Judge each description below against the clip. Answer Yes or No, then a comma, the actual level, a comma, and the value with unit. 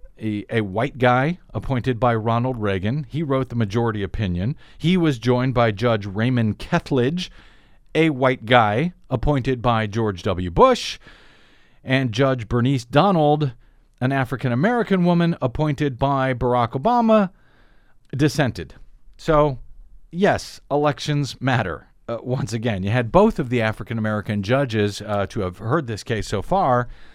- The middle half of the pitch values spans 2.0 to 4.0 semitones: No, average, 4.4 semitones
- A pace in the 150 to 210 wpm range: No, average, 140 wpm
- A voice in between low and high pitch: No, low, 125 Hz